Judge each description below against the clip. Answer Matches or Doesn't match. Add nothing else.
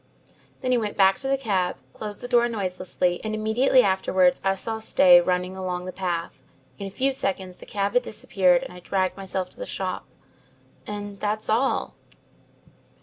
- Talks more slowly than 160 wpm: Doesn't match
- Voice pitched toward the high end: Matches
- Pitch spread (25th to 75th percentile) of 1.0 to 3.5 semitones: Matches